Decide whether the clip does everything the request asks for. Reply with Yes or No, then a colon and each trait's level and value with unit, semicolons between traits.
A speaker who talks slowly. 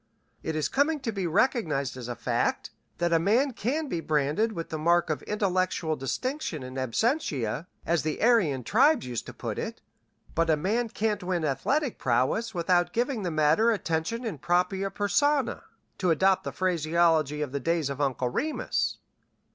No: average, 170 wpm